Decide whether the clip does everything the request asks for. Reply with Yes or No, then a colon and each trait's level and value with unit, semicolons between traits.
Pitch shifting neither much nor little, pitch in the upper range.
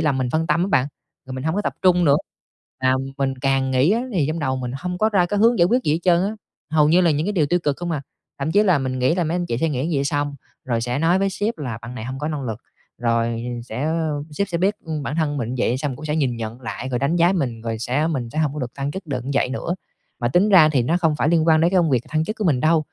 No: average, 4.8 semitones; medium, 150 Hz